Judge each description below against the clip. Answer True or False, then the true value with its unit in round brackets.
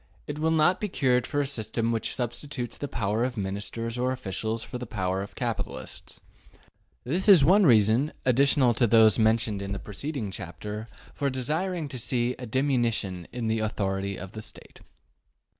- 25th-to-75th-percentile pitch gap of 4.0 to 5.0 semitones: True (4.4 semitones)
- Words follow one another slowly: False (175 wpm)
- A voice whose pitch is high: False (120 Hz)